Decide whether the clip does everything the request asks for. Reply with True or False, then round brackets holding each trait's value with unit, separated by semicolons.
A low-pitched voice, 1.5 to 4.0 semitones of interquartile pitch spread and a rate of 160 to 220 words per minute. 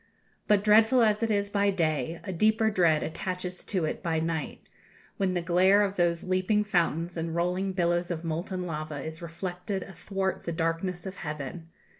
False (180 Hz; 2.9 semitones; 175 wpm)